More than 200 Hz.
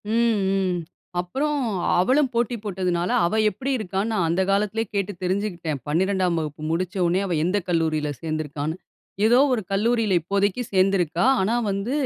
No: high, 190 Hz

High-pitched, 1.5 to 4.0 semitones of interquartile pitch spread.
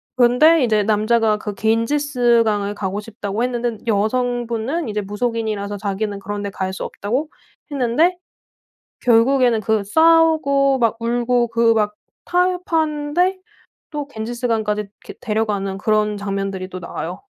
Yes: high, 230 Hz; average, 3.6 semitones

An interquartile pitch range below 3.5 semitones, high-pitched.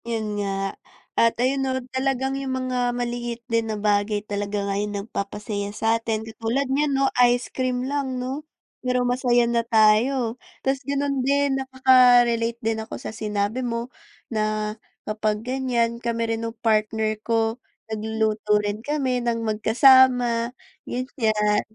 Yes: average, 2.9 semitones; high, 235 Hz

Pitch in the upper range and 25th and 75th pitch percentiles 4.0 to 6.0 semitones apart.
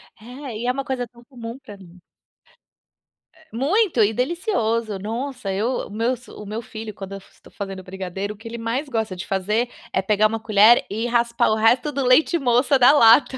No: high, 230 Hz; average, 3.3 semitones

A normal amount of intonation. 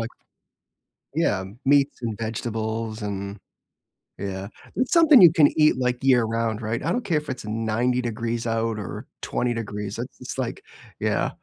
Yes: average, 3.1 semitones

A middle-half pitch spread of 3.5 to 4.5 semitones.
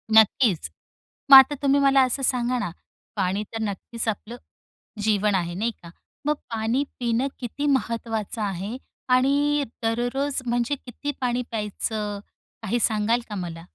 Yes: average, 3.8 semitones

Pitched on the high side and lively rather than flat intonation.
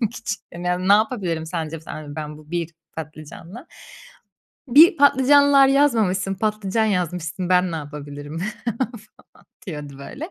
No: medium, 180 Hz; wide, 6.3 semitones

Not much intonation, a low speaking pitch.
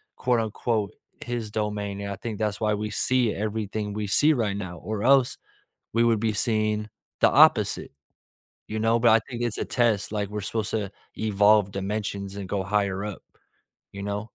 Yes: narrow, 1.8 semitones; low, 105 Hz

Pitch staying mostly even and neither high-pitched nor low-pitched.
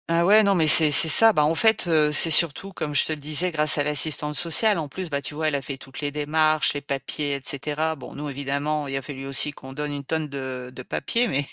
Yes: narrow, 2.2 semitones; medium, 150 Hz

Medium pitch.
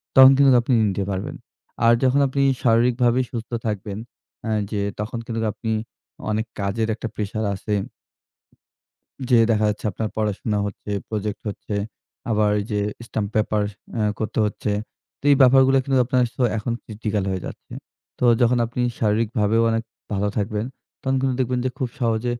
No: low, 110 Hz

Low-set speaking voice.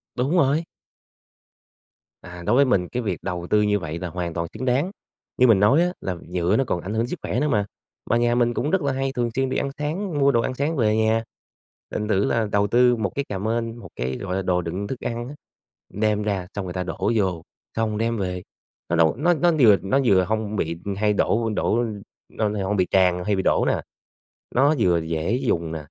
Yes: low, 105 Hz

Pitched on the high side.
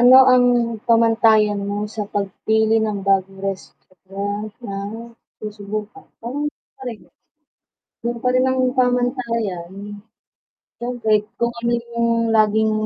Yes: high, 220 Hz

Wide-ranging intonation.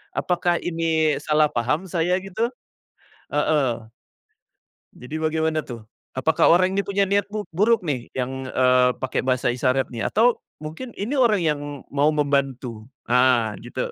Yes: wide, 6.0 semitones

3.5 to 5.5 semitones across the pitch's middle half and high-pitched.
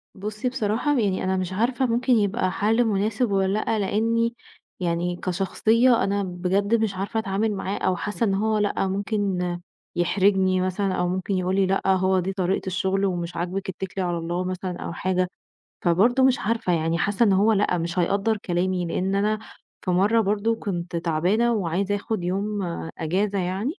No: average, 2.7 semitones; high, 195 Hz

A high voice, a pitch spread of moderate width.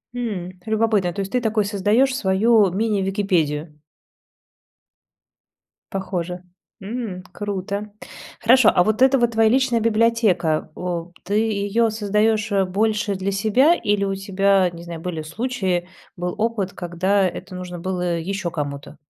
Yes: high, 200 Hz; average, 3.5 semitones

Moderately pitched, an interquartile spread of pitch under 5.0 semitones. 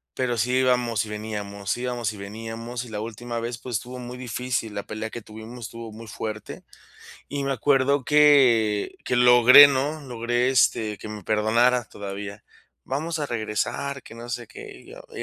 No: low, 120 Hz; average, 2.8 semitones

